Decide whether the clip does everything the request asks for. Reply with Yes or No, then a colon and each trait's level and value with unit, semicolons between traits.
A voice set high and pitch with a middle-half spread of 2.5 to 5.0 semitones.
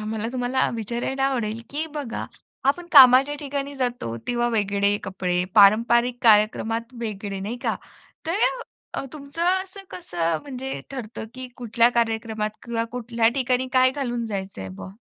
Yes: high, 235 Hz; average, 3.6 semitones